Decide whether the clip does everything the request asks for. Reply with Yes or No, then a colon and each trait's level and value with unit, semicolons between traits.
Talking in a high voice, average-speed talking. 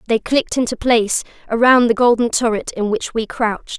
Yes: high, 230 Hz; average, 190 wpm